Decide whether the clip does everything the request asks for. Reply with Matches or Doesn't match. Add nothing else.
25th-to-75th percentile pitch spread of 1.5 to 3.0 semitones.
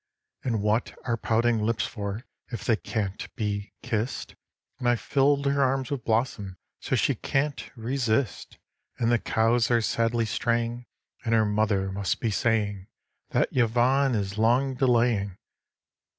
Matches